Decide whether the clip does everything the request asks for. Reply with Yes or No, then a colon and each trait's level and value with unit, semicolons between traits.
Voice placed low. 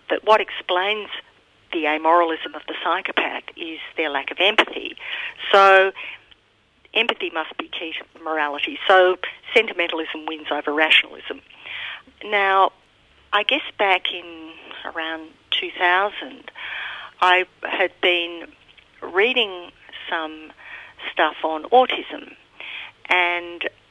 No: medium, 180 Hz